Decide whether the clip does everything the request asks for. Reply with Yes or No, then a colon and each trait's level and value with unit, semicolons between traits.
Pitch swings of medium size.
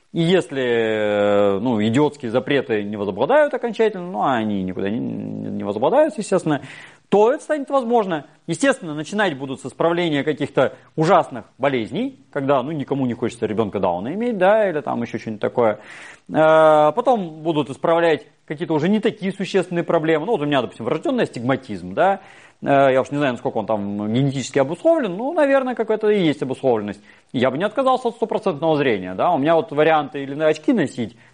No: wide, 7.2 semitones